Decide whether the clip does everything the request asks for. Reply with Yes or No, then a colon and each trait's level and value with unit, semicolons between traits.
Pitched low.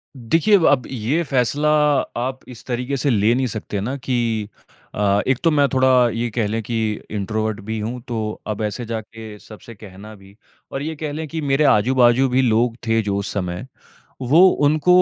Yes: low, 120 Hz